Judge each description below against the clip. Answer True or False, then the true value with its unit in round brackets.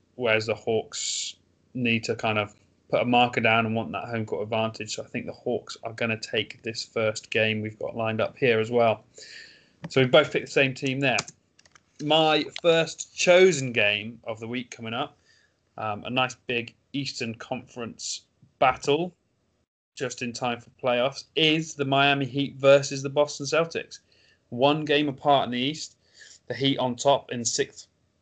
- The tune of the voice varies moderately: True (3.8 semitones)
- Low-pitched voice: True (125 Hz)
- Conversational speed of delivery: True (180 wpm)